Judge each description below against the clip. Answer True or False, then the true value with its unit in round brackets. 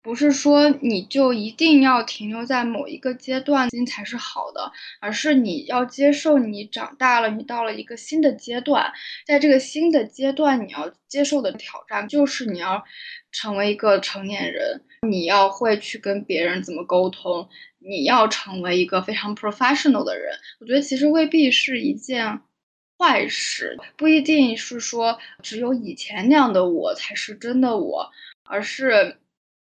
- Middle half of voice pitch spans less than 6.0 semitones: True (5.3 semitones)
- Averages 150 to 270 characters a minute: True (265 characters per minute)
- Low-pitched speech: False (250 Hz)